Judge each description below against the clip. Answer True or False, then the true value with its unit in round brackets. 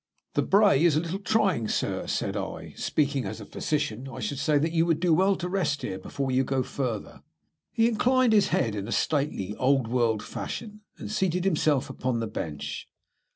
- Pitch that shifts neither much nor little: False (7.1 semitones)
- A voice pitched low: False (145 Hz)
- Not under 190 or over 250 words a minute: True (200 wpm)